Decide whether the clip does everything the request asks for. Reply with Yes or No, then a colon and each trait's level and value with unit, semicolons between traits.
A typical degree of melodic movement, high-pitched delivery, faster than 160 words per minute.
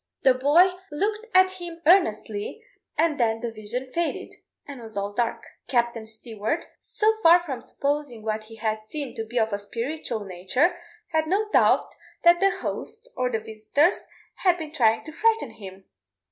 No: wide, 7.5 semitones; very high, 255 Hz; average, 170 wpm